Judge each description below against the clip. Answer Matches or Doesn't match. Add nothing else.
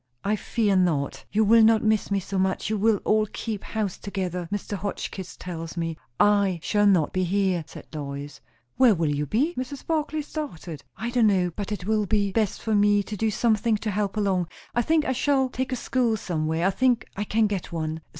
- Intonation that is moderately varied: Matches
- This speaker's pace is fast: Matches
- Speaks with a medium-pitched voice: Doesn't match